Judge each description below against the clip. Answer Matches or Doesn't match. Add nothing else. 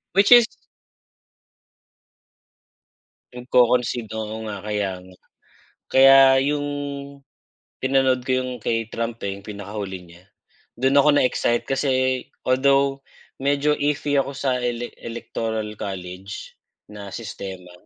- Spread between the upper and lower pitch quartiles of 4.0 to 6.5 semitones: Matches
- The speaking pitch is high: Doesn't match